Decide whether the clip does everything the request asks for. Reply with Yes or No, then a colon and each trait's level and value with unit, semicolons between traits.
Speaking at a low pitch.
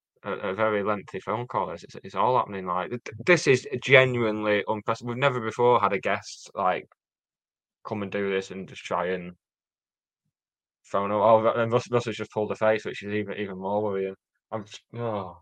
Yes: low, 105 Hz